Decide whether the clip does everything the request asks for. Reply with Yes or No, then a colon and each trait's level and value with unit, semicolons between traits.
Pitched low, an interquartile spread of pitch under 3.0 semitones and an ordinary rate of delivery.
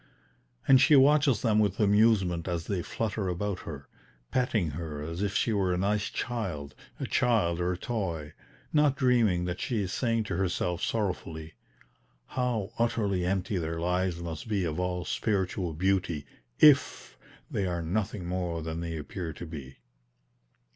No: very low, 95 Hz; average, 4.3 semitones; average, 160 wpm